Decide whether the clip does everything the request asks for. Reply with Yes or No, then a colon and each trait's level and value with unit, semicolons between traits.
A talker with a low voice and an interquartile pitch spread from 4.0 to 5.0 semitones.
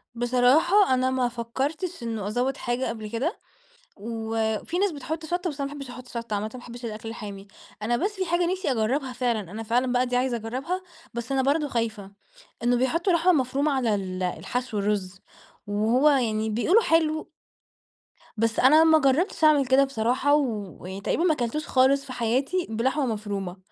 No: very high, 250 Hz; average, 4.6 semitones